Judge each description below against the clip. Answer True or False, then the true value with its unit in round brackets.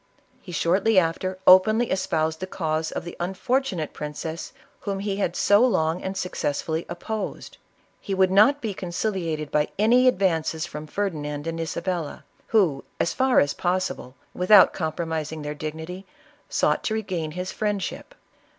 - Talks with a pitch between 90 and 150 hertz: False (180 Hz)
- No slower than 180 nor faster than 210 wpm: False (150 wpm)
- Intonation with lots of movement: False (3.9 semitones)